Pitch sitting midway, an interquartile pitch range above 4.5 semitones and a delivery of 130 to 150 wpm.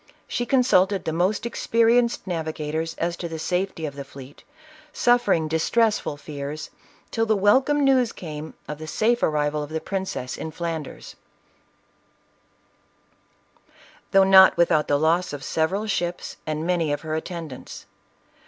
Yes: medium, 170 Hz; average, 4.9 semitones; average, 145 wpm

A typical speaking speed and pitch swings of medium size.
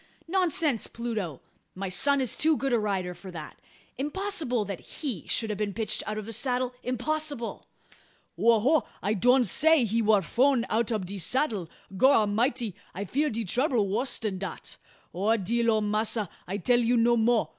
Yes: average, 175 wpm; average, 4.1 semitones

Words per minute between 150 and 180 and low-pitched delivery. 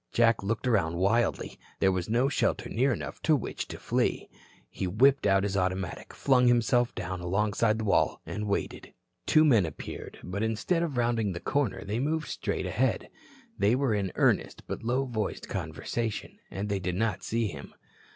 Yes: average, 175 wpm; low, 110 Hz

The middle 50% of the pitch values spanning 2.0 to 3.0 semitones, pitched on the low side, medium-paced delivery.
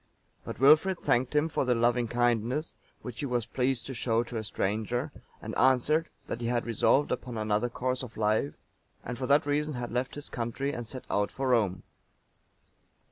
Yes: narrow, 2.6 semitones; low, 125 Hz; average, 190 wpm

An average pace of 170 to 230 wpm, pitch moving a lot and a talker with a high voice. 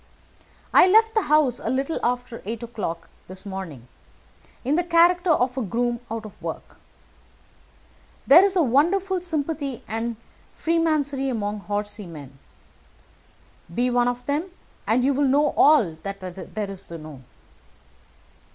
No: average, 140 wpm; wide, 6.9 semitones; high, 245 Hz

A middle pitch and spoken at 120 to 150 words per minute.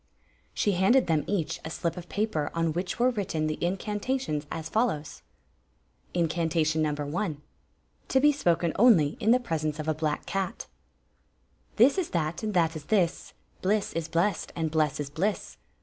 No: medium, 170 Hz; average, 165 wpm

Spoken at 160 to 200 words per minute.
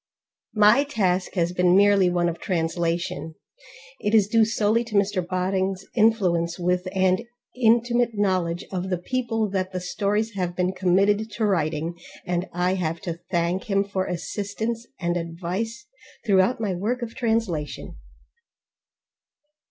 No: average, 140 wpm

